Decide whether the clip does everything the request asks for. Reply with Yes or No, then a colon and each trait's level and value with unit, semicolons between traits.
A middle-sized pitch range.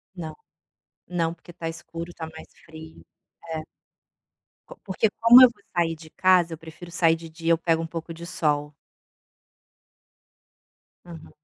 No: narrow, 1.3 semitones